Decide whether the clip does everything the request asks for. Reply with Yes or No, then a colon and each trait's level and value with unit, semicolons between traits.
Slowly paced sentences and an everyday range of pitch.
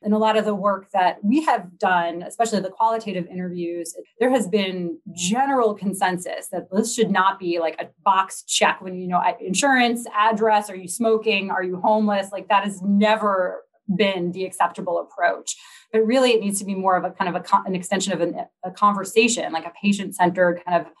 No: fast, 205 wpm; average, 3.1 semitones